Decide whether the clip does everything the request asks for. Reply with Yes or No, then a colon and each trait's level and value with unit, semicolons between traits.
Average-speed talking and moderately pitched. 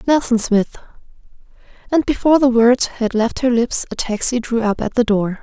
No: average, 190 wpm; high, 240 Hz